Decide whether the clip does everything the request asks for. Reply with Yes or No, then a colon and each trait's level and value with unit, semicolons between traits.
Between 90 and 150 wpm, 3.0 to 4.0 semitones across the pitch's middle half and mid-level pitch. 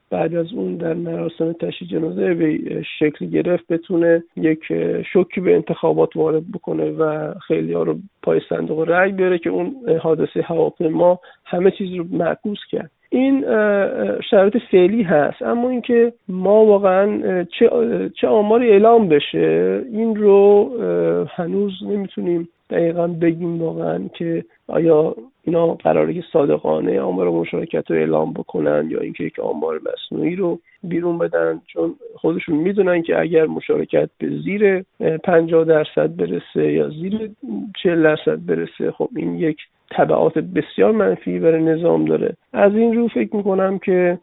No: average, 140 wpm; average, 4.5 semitones; medium, 175 Hz